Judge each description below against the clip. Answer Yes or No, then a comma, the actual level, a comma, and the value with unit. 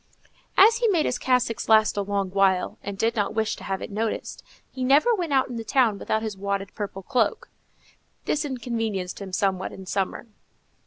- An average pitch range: Yes, average, 4.3 semitones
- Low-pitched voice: No, high, 220 Hz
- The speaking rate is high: No, average, 195 wpm